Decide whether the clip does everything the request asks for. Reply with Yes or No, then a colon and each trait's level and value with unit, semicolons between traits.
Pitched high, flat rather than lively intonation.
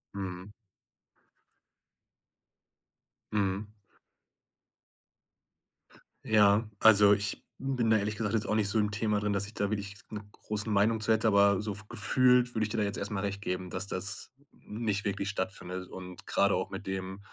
No: low, 100 Hz; narrow, 1.6 semitones